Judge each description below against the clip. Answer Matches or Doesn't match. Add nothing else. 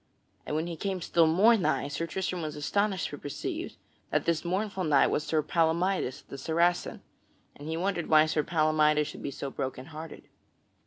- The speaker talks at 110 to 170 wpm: Doesn't match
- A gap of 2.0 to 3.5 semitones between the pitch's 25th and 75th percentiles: Matches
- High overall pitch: Doesn't match